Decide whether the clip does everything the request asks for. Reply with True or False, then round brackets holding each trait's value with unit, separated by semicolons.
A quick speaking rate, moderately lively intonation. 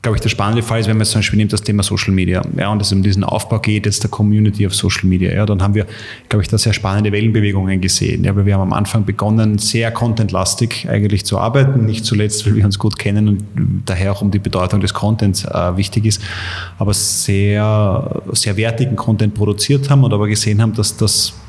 False (235 wpm; 1.8 semitones)